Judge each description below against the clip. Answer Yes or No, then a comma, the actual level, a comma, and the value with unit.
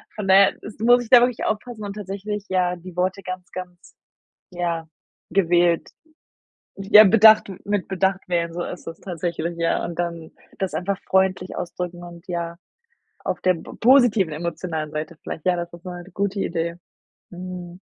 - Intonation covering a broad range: No, narrow, 2.5 semitones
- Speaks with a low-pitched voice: No, medium, 180 Hz